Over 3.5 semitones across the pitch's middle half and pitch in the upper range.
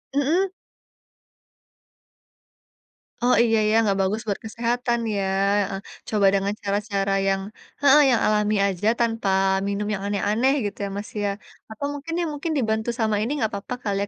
No: average, 3.0 semitones; high, 210 Hz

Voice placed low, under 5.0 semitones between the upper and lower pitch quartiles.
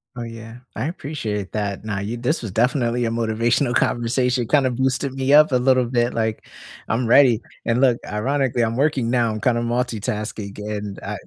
Yes: low, 120 Hz; narrow, 2.6 semitones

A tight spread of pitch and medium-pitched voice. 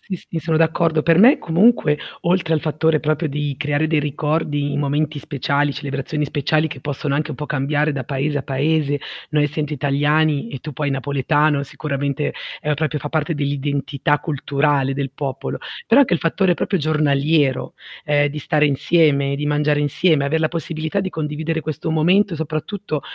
Yes: narrow, 1.8 semitones; medium, 150 Hz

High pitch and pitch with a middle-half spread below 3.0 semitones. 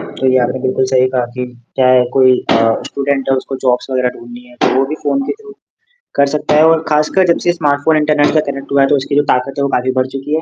No: low, 135 Hz; narrow, 2.6 semitones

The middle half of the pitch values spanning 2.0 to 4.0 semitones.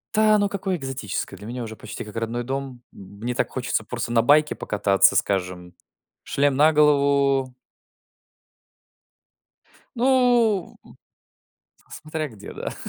No: wide, 5.4 semitones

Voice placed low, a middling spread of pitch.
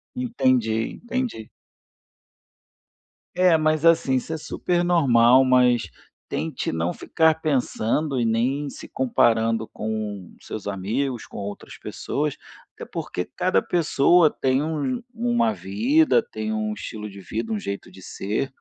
No: low, 130 Hz; wide, 7.3 semitones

